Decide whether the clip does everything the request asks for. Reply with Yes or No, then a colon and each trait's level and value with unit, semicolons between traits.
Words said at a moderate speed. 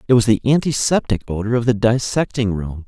Yes: average, 190 wpm